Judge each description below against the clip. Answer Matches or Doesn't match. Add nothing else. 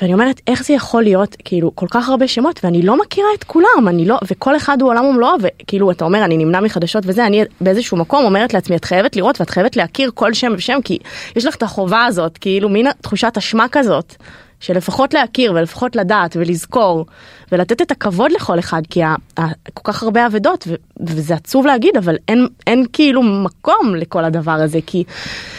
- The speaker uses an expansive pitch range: Matches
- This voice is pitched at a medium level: Doesn't match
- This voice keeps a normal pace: Doesn't match